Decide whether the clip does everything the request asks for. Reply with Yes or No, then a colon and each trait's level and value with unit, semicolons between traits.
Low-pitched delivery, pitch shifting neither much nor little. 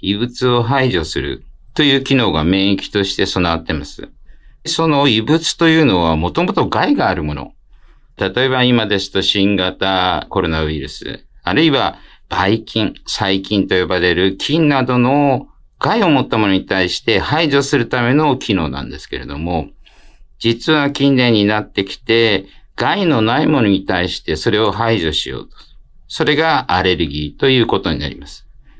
No: low, 105 Hz; wide, 6.6 semitones